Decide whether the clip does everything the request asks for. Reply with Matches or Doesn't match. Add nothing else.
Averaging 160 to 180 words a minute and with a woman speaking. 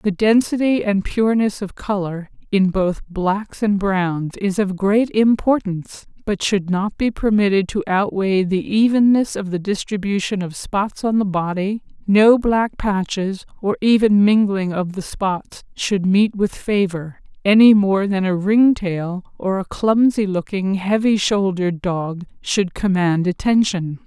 Doesn't match